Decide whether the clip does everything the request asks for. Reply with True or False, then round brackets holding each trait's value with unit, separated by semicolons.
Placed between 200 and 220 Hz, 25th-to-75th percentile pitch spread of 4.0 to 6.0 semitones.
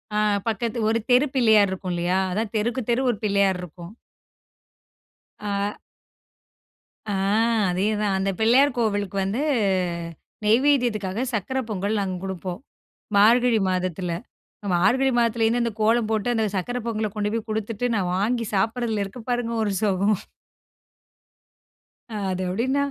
False (215 Hz; 3.4 semitones)